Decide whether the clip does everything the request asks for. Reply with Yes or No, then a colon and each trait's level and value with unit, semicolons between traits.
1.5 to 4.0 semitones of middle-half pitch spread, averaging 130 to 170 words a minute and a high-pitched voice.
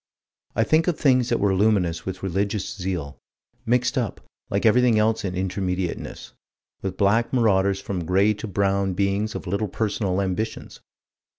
No: average, 2.7 semitones; average, 160 wpm; low, 100 Hz